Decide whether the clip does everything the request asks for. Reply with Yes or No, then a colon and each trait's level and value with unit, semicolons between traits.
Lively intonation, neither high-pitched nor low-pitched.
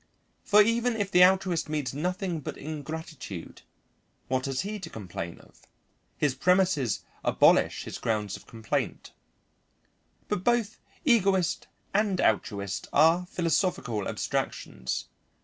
Yes: wide, 6.9 semitones; medium, 165 Hz